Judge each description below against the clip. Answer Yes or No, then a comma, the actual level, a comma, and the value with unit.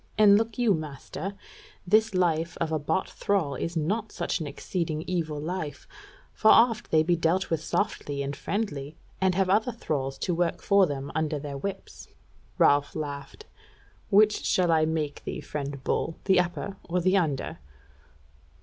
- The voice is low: No, medium, 165 Hz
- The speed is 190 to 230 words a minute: No, average, 165 wpm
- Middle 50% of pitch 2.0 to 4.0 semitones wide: No, average, 4.7 semitones